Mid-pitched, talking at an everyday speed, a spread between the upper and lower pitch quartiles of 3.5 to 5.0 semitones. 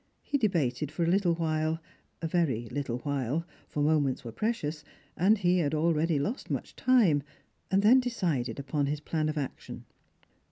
Yes: medium, 155 Hz; average, 175 wpm; average, 4.1 semitones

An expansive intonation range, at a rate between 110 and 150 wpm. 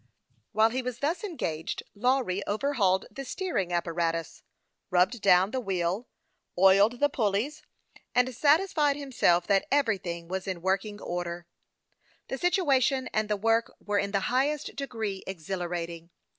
Yes: wide, 6.5 semitones; average, 140 wpm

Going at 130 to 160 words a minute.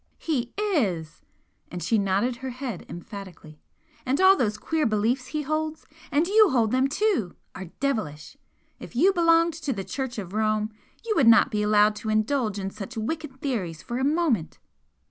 No: average, 175 wpm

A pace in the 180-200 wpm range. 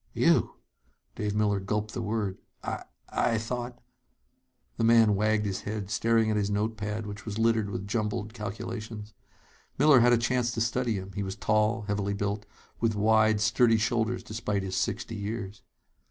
No: average, 170 wpm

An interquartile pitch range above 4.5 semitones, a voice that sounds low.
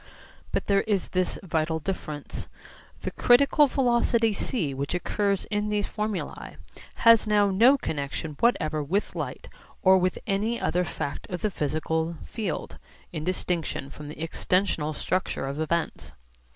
No: average, 5.2 semitones; medium, 185 Hz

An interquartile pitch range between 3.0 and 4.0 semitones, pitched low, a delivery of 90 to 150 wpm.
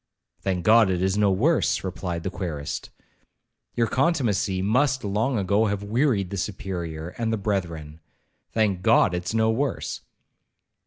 Yes: average, 3.5 semitones; low, 100 Hz; average, 140 wpm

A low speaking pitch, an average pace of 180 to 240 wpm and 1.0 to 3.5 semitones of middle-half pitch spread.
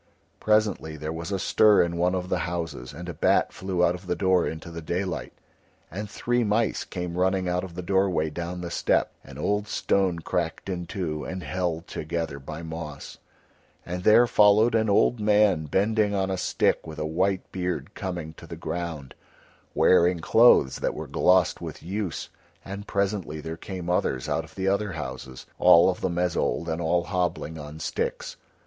Yes: very low, 90 Hz; average, 185 wpm; average, 3.2 semitones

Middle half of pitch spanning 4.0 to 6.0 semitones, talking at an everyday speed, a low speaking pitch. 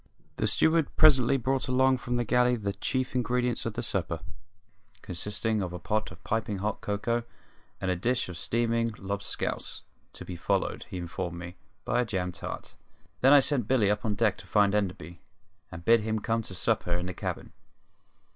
Yes: average, 4.6 semitones; average, 185 wpm; low, 110 Hz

